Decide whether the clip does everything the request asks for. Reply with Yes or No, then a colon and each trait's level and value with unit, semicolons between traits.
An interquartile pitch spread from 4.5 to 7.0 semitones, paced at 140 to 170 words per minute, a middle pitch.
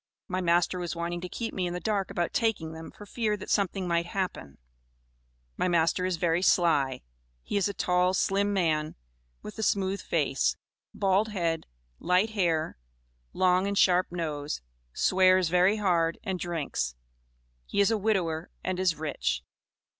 No: average, 2.8 semitones; average, 160 wpm; medium, 180 Hz